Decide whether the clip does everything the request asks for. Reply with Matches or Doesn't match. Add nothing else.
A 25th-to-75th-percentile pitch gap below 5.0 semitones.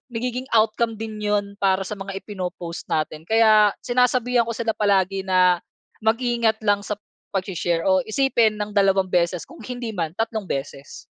Matches